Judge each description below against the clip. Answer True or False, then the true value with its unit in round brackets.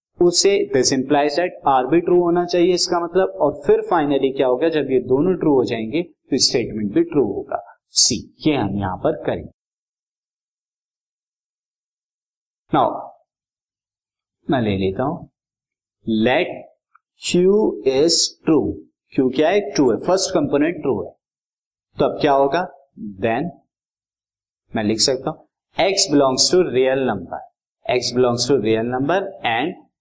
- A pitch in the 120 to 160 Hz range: True (140 Hz)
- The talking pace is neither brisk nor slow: True (140 wpm)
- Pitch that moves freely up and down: True (6.4 semitones)